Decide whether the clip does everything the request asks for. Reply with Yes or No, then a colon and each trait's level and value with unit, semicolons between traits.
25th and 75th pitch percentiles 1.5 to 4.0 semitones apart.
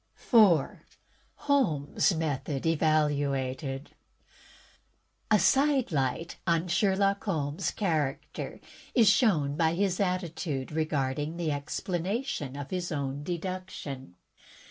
No: average, 4.8 semitones